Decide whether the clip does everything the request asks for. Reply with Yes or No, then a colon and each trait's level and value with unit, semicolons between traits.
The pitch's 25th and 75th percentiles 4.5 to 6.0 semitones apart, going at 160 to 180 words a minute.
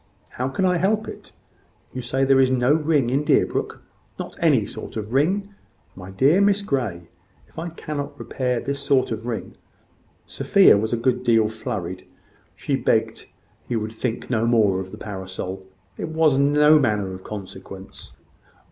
Yes: wide, 5.5 semitones; average, 170 wpm